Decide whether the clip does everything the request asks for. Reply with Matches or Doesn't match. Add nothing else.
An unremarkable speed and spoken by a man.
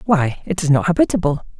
Doesn't match